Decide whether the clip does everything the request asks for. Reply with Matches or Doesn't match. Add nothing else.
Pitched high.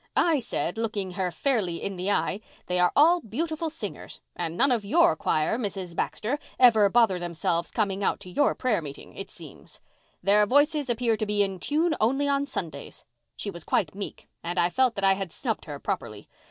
Matches